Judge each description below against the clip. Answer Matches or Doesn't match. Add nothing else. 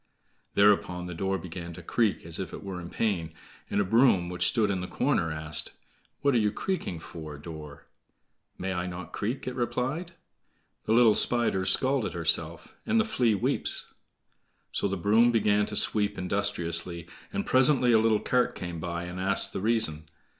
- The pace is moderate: Matches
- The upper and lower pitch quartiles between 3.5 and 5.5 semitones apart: Matches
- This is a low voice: Matches